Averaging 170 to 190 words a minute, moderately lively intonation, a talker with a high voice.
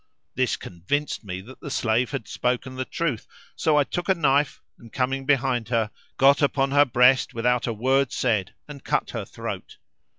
No: average, 185 wpm; average, 3.0 semitones; low, 130 Hz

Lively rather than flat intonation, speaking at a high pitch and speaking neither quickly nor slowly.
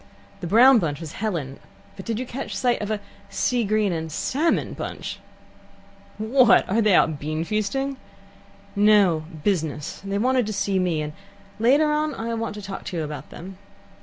Yes: wide, 5.7 semitones; high, 205 Hz; average, 170 wpm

